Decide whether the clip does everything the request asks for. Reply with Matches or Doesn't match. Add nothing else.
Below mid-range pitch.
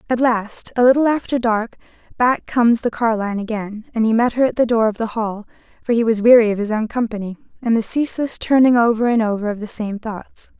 Doesn't match